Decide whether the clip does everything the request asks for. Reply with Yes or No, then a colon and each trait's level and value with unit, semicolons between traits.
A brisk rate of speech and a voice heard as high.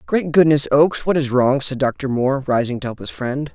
No: fast, 235 wpm; low, 135 Hz